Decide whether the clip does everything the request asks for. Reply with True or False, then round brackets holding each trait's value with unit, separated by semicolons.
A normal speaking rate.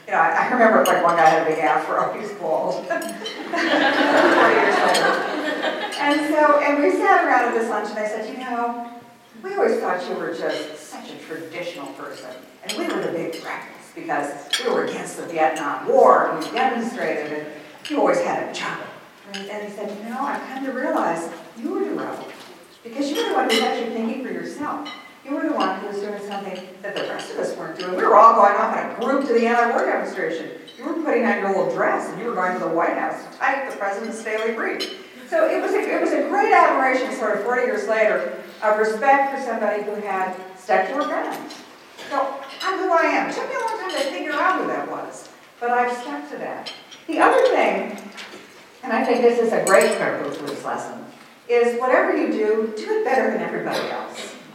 False (220 wpm)